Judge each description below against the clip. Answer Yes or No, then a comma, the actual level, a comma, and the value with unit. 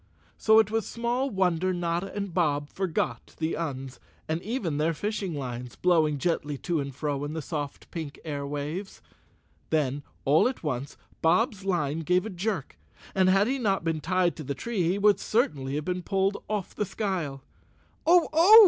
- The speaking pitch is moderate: Yes, medium, 175 Hz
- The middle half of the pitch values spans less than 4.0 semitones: No, average, 5.3 semitones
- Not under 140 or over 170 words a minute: No, average, 180 wpm